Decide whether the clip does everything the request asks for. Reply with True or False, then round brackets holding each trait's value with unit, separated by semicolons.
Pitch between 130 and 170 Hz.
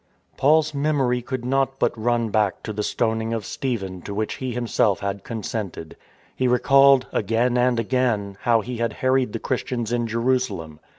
False (120 Hz)